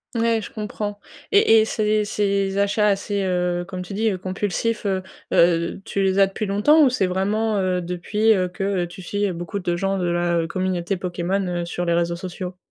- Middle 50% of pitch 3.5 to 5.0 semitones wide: No, narrow, 2.6 semitones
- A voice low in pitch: No, high, 195 Hz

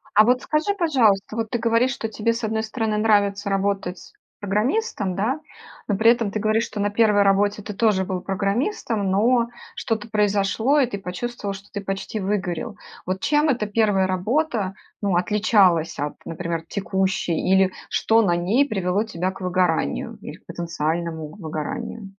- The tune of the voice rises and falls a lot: No, average, 3.2 semitones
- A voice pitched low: No, high, 205 Hz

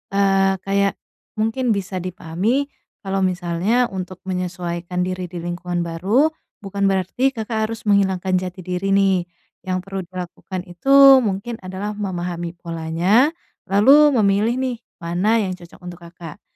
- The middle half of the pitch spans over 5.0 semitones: No, average, 3.0 semitones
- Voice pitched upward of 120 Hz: Yes, high, 190 Hz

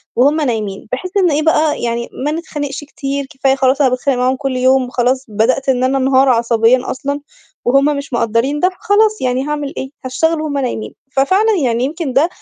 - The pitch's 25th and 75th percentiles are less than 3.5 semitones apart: Yes, average, 2.8 semitones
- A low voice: No, very high, 270 Hz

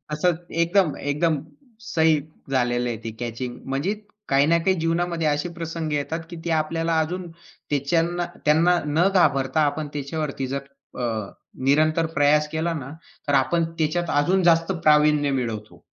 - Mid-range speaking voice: Yes, medium, 155 Hz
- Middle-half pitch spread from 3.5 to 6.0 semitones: No, average, 3.1 semitones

